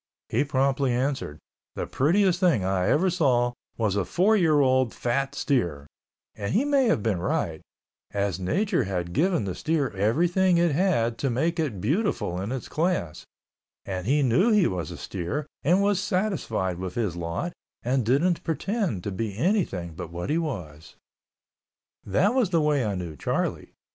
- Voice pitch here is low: Yes, low, 130 Hz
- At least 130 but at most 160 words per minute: No, average, 170 wpm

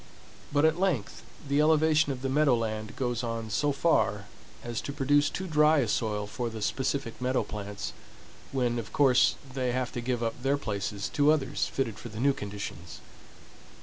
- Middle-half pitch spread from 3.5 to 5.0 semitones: Yes, average, 4.5 semitones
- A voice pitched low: Yes, low, 125 Hz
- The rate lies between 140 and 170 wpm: No, average, 180 wpm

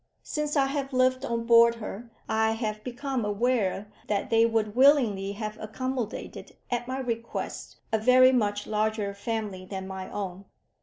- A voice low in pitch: No, high, 225 Hz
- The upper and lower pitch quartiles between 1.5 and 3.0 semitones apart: No, average, 3.5 semitones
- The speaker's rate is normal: Yes, average, 155 wpm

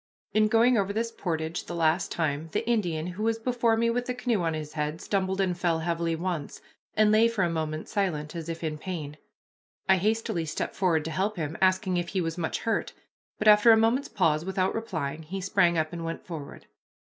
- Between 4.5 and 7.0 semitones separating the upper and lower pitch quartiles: Yes, average, 4.9 semitones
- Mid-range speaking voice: Yes, medium, 180 Hz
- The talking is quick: Yes, fast, 215 wpm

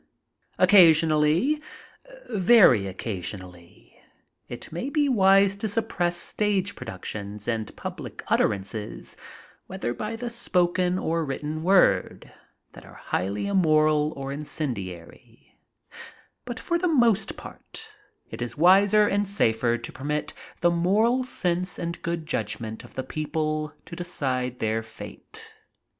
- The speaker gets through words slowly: Yes, slow, 125 wpm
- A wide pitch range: Yes, wide, 8.6 semitones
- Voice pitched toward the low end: No, medium, 165 Hz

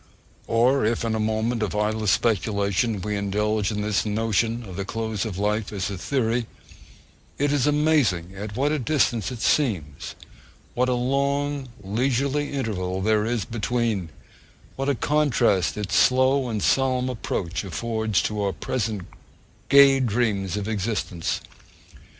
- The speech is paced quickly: No, average, 145 wpm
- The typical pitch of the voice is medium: No, low, 110 Hz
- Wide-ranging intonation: No, average, 3.9 semitones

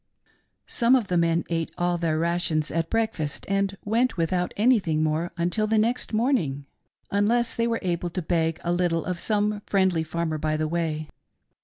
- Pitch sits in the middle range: Yes, medium, 175 Hz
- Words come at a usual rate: Yes, average, 170 wpm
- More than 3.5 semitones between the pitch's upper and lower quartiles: Yes, average, 4.5 semitones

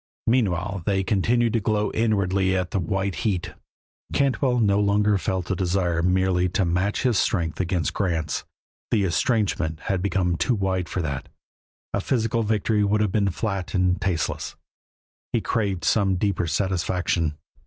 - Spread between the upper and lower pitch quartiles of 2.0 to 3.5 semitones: Yes, average, 2.8 semitones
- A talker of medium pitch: No, very low, 95 Hz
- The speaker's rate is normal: Yes, average, 155 wpm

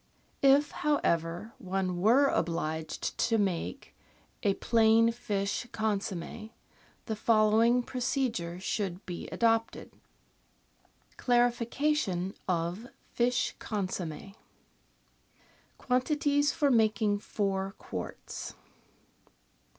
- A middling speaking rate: No, slow, 85 wpm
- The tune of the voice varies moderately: Yes, average, 4.4 semitones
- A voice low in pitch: No, high, 220 Hz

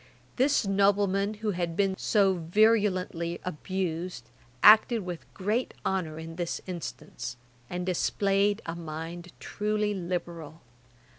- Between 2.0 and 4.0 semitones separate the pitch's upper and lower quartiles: Yes, average, 3.2 semitones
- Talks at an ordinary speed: No, slow, 115 wpm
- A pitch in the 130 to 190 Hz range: Yes, medium, 185 Hz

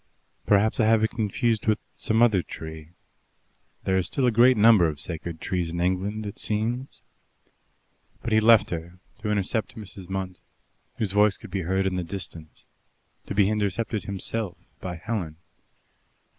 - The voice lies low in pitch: Yes, low, 100 Hz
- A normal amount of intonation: Yes, average, 3.3 semitones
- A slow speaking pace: No, average, 160 wpm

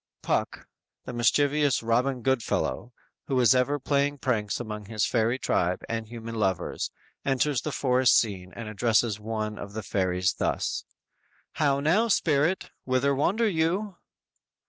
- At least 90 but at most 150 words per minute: Yes, average, 145 wpm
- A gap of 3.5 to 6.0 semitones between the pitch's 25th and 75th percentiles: Yes, average, 4.7 semitones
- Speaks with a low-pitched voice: Yes, low, 125 Hz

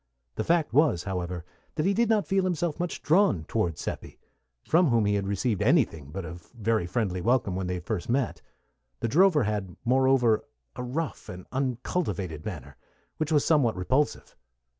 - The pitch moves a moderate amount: No, wide, 8.6 semitones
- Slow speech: No, average, 170 wpm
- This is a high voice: No, low, 115 Hz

